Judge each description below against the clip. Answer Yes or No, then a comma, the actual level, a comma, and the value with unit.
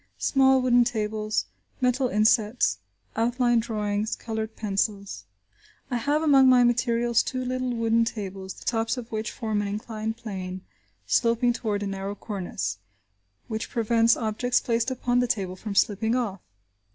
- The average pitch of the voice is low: No, high, 225 Hz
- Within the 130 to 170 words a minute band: Yes, average, 145 wpm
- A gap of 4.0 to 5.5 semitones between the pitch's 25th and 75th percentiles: No, average, 2.7 semitones